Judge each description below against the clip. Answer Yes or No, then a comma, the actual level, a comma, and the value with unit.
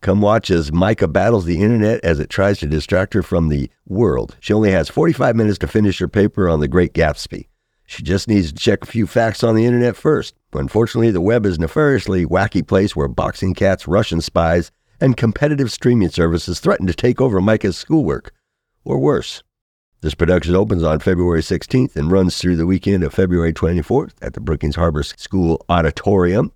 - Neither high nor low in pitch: No, very low, 95 Hz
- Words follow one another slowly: No, average, 195 wpm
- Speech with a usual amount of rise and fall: Yes, average, 4.4 semitones